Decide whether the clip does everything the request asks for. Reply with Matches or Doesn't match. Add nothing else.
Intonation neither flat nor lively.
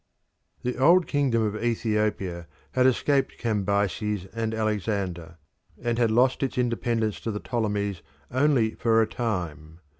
Matches